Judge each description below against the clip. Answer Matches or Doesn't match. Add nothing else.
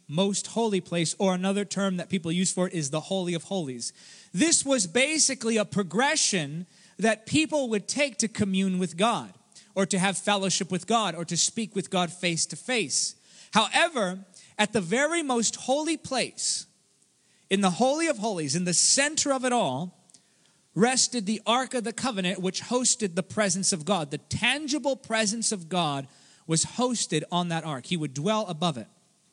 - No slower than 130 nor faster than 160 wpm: Doesn't match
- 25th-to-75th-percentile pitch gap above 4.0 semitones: Matches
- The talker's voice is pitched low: Doesn't match